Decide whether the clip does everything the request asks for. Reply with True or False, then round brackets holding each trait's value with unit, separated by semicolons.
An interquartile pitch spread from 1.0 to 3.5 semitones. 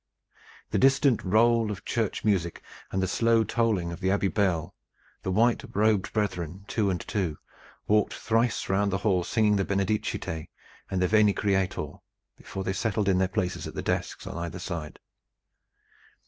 True (2.9 semitones)